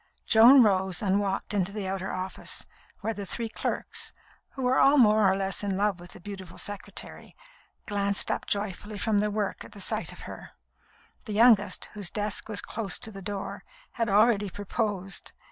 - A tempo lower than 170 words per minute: No, average, 180 wpm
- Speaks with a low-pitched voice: No, high, 205 Hz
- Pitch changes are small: Yes, narrow, 1.9 semitones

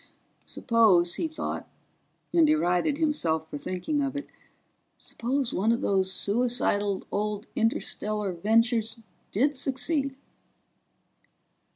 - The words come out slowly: Yes, slow, 90 wpm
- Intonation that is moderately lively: No, wide, 6.0 semitones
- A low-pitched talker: No, high, 225 Hz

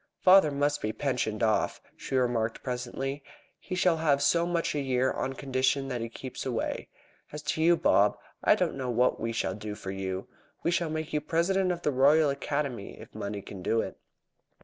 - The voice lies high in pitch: No, low, 135 Hz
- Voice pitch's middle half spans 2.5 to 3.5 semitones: No, average, 5.0 semitones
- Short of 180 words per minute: No, average, 195 wpm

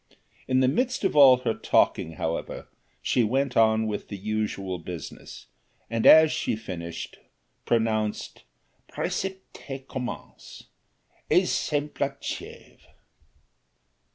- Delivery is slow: Yes, slow, 100 wpm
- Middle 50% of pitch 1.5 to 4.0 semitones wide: No, average, 4.7 semitones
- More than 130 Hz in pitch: No, low, 115 Hz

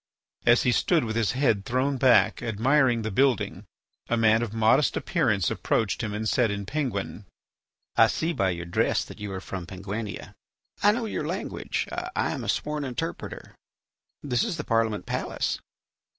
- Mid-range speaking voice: No, low, 115 Hz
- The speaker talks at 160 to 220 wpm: Yes, average, 170 wpm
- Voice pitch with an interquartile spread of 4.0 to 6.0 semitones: Yes, average, 4.6 semitones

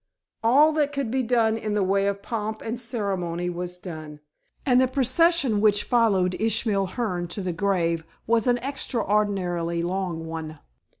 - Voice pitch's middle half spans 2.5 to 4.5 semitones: No, average, 5.1 semitones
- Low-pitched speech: No, high, 205 Hz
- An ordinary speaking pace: Yes, average, 160 wpm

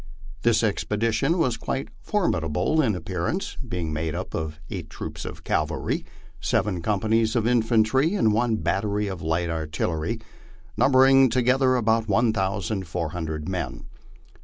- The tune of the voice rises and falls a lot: Yes, wide, 5.9 semitones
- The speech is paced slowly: Yes, slow, 130 wpm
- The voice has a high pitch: No, low, 105 Hz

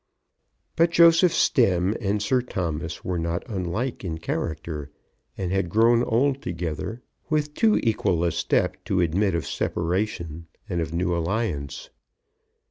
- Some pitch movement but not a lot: No, wide, 5.7 semitones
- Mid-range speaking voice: No, very low, 90 Hz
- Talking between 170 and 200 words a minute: No, slow, 135 wpm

